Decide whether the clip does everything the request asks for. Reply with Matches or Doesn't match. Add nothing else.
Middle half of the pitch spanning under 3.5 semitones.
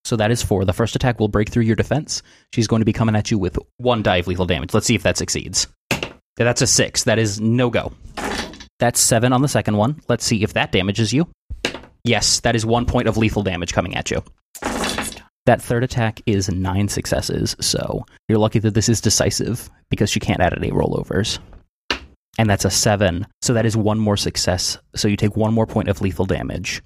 Matches